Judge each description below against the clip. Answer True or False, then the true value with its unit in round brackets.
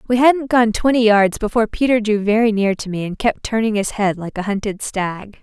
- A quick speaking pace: True (230 wpm)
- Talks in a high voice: True (215 Hz)